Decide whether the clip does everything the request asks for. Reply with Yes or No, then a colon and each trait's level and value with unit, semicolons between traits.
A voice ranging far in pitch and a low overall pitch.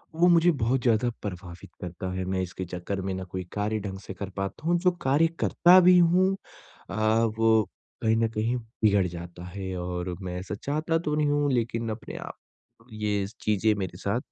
Yes: wide, 6.8 semitones; low, 105 Hz